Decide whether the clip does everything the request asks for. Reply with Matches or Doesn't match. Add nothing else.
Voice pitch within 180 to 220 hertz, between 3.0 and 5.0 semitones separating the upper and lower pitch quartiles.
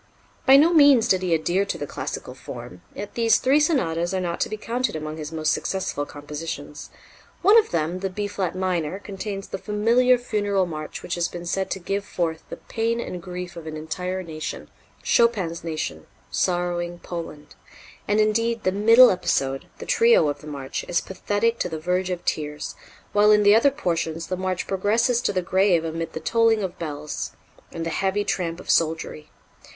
Matches